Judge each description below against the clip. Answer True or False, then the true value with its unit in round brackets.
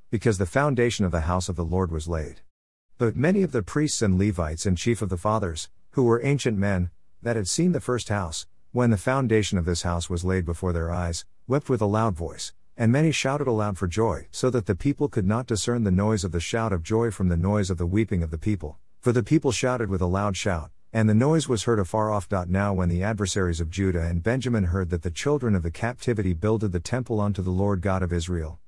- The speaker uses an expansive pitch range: False (4.7 semitones)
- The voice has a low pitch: True (105 Hz)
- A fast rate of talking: True (245 wpm)